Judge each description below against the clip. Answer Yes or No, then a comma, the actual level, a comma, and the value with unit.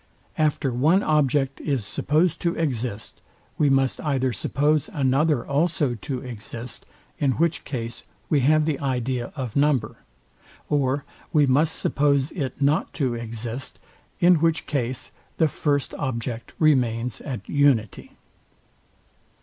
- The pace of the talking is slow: Yes, slow, 125 wpm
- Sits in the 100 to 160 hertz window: Yes, low, 135 Hz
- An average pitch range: Yes, average, 3.5 semitones